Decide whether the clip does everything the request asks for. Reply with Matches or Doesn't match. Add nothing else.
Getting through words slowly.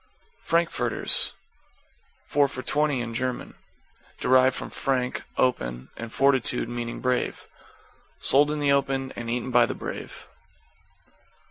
Matches